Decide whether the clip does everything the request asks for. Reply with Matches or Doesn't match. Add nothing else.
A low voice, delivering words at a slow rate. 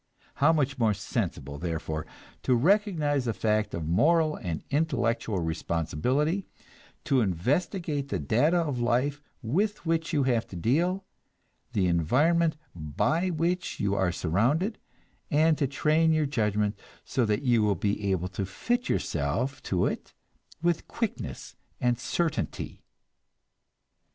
Matches